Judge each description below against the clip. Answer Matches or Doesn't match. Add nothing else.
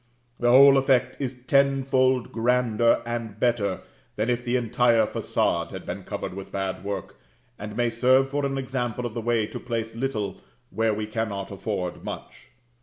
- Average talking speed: Matches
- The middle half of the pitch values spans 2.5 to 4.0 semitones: Matches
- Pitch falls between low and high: Doesn't match